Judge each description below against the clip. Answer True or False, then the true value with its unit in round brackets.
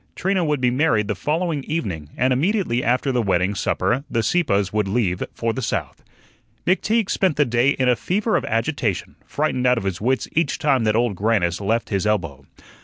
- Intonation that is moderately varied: False (6.3 semitones)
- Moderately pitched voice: False (120 Hz)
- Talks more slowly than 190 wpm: False (195 wpm)